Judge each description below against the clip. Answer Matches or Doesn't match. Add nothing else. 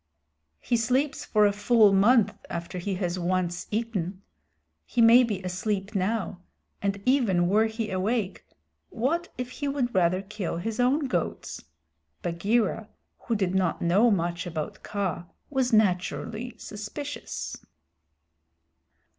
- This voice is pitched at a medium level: Doesn't match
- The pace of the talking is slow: Matches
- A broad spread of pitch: Doesn't match